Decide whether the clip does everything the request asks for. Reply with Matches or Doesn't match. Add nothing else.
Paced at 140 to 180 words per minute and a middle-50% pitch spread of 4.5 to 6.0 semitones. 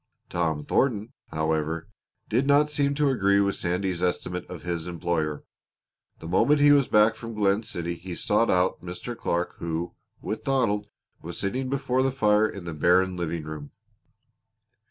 Matches